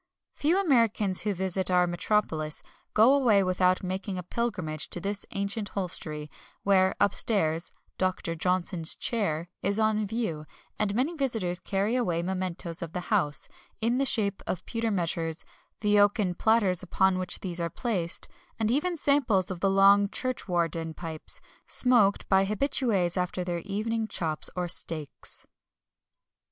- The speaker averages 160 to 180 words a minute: No, average, 145 wpm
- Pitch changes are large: No, average, 3.9 semitones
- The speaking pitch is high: Yes, high, 195 Hz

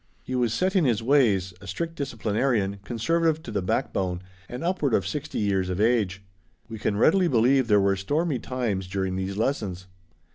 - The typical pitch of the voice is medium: No, low, 115 Hz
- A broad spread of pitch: Yes, wide, 6.1 semitones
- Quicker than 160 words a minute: Yes, average, 180 wpm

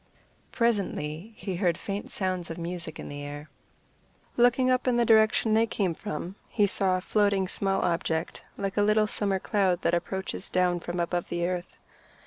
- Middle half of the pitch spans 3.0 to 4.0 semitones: Yes, average, 3.5 semitones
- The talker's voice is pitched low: No, high, 190 Hz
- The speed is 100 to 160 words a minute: No, average, 175 wpm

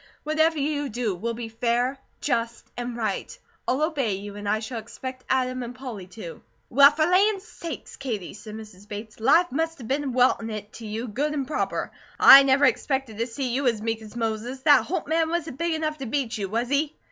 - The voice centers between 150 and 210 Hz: No, very high, 250 Hz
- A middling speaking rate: No, fast, 210 wpm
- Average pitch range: Yes, average, 4.7 semitones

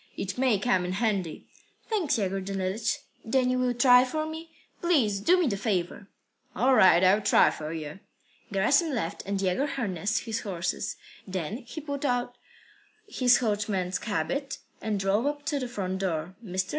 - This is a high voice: Yes, high, 215 Hz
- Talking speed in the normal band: Yes, average, 170 wpm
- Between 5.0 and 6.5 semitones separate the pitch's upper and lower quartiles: Yes, wide, 5.4 semitones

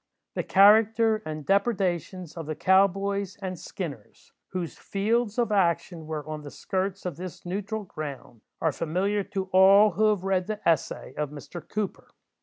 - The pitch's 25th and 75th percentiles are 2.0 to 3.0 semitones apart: No, average, 3.7 semitones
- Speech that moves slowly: No, average, 165 wpm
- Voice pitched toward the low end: No, high, 190 Hz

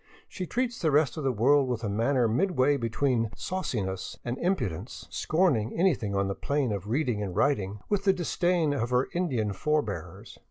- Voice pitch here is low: Yes, low, 130 Hz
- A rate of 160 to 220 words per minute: Yes, average, 185 wpm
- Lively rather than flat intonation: Yes, wide, 6.8 semitones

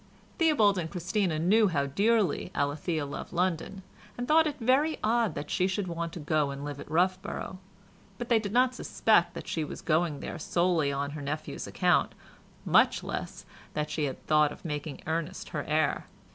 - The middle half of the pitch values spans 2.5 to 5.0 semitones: No, wide, 5.4 semitones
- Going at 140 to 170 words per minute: No, average, 185 wpm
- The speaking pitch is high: No, medium, 170 Hz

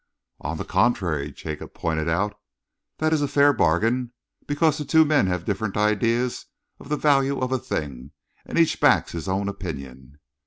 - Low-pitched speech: Yes, low, 105 Hz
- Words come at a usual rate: Yes, average, 170 wpm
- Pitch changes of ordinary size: No, wide, 9.0 semitones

